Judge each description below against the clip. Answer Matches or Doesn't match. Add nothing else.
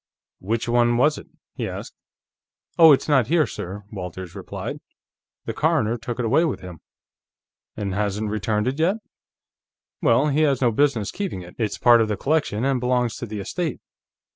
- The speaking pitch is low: Matches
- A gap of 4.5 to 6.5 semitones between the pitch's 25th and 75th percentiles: Matches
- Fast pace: Doesn't match